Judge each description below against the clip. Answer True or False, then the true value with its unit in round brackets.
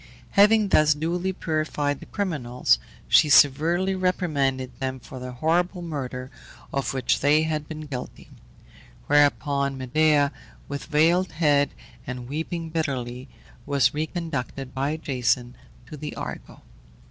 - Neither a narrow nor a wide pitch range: True (3.3 semitones)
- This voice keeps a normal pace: False (125 wpm)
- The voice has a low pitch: False (145 Hz)